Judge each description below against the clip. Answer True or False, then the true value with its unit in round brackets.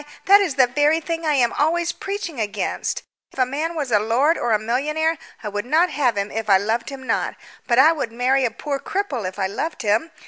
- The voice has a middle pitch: False (265 Hz)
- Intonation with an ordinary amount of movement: False (5.9 semitones)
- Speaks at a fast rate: True (235 wpm)